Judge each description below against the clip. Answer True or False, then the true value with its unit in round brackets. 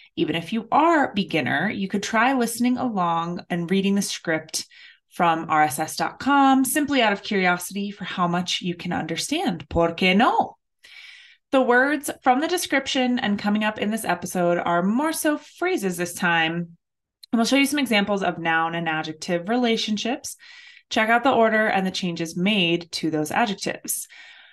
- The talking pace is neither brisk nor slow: True (165 wpm)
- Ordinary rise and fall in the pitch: False (6.9 semitones)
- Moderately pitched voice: False (205 Hz)